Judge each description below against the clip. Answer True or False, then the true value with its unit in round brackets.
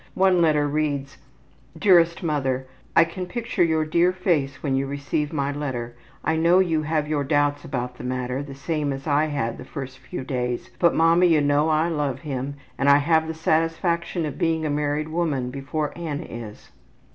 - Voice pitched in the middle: True (150 Hz)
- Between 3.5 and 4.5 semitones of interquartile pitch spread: False (3.1 semitones)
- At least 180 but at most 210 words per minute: True (190 wpm)